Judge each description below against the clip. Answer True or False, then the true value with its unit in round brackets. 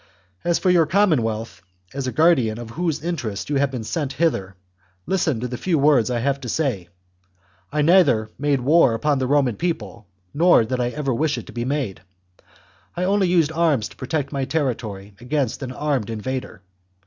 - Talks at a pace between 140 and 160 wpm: False (185 wpm)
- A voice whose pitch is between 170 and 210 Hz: False (135 Hz)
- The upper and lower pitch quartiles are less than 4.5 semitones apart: False (5.0 semitones)